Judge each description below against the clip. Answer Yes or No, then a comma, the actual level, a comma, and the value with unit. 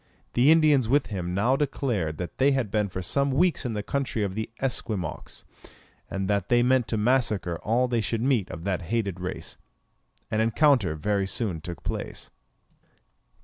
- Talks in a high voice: No, low, 110 Hz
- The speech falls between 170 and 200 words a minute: Yes, average, 175 wpm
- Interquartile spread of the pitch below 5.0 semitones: No, wide, 5.6 semitones